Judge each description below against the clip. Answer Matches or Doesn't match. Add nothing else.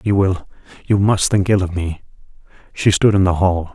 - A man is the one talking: Matches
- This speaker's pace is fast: Doesn't match